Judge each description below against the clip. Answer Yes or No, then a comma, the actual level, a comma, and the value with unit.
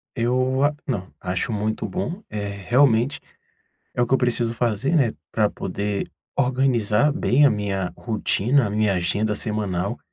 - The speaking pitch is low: Yes, low, 115 Hz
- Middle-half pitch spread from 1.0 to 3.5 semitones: No, average, 4.1 semitones